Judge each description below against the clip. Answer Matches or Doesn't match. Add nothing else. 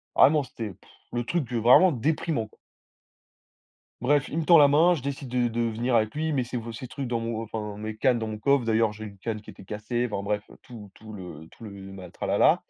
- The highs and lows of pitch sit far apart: Doesn't match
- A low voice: Matches